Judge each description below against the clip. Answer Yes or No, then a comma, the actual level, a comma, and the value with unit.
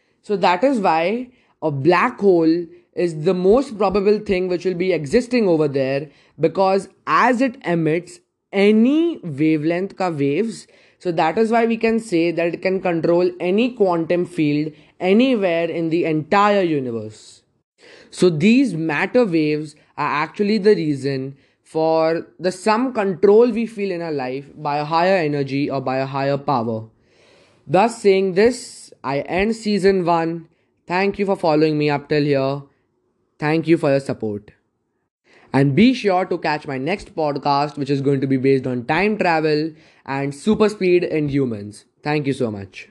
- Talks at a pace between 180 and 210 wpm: No, average, 165 wpm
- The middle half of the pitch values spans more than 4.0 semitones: Yes, average, 5.2 semitones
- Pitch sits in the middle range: Yes, medium, 170 Hz